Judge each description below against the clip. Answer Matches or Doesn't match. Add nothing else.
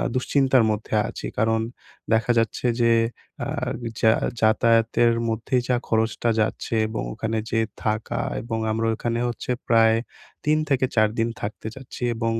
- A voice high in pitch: Doesn't match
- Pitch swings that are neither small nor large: Doesn't match